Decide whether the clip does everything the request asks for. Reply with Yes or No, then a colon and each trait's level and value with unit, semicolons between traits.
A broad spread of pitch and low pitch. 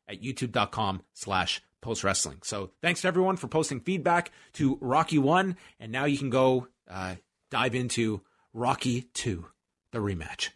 Yes: wide, 6.3 semitones; low, 125 Hz